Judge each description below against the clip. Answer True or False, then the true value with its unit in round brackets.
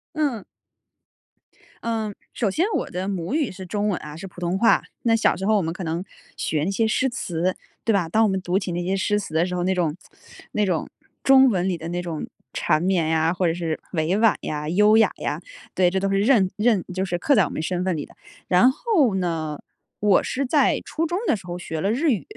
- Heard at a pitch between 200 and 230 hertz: False (190 Hz)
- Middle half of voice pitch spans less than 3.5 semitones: False (3.9 semitones)